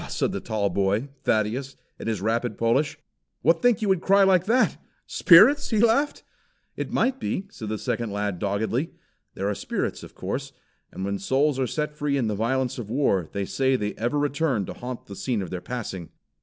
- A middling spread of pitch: No, wide, 6.7 semitones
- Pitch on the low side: Yes, low, 125 Hz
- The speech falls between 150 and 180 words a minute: No, average, 200 wpm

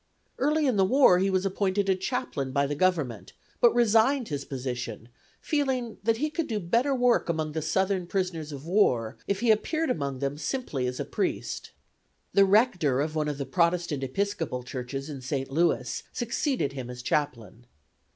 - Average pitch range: No, wide, 8.4 semitones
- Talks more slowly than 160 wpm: No, average, 180 wpm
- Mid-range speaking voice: Yes, medium, 170 Hz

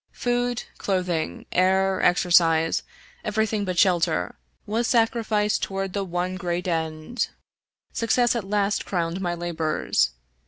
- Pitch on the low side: No, high, 190 Hz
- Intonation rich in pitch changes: No, average, 3.5 semitones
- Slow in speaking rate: Yes, slow, 120 wpm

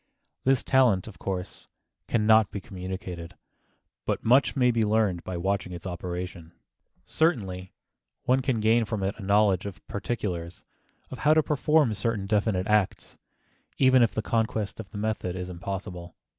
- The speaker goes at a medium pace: Yes, average, 155 wpm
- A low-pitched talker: Yes, low, 105 Hz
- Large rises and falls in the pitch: No, average, 3.8 semitones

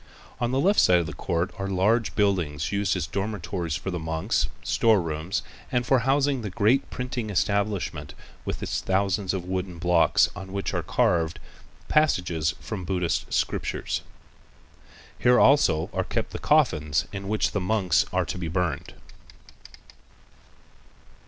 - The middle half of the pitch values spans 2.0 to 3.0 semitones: No, average, 4.0 semitones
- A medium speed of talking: Yes, average, 150 wpm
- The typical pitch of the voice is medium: No, very low, 95 Hz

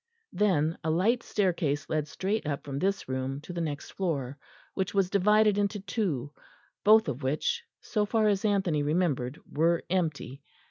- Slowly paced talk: No, average, 165 wpm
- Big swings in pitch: Yes, wide, 5.7 semitones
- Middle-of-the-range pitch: Yes, medium, 175 Hz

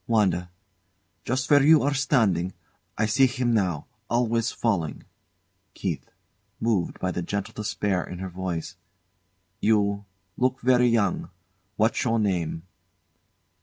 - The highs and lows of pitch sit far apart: No, average, 4.9 semitones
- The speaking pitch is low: Yes, low, 105 Hz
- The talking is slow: Yes, slow, 125 wpm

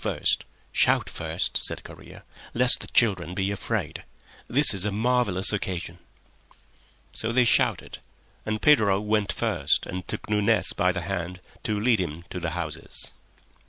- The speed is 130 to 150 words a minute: Yes, average, 145 wpm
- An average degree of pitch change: Yes, average, 3.5 semitones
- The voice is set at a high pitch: No, low, 100 Hz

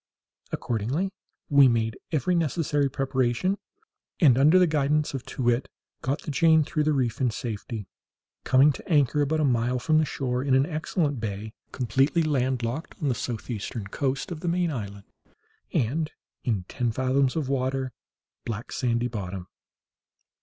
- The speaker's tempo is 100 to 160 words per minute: Yes, average, 155 wpm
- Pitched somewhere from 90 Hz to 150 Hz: Yes, low, 135 Hz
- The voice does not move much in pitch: No, average, 4.2 semitones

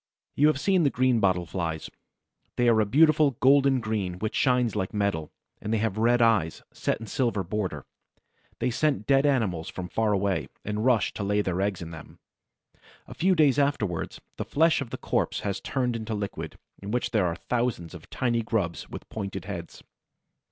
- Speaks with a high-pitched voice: No, low, 110 Hz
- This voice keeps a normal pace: Yes, average, 185 wpm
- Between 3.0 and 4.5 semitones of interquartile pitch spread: No, average, 5.1 semitones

